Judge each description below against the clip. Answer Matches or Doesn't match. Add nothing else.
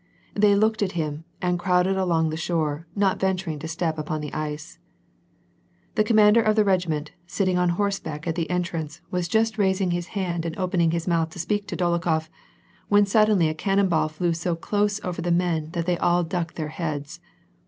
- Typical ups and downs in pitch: Matches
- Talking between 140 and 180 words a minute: Doesn't match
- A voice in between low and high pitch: Matches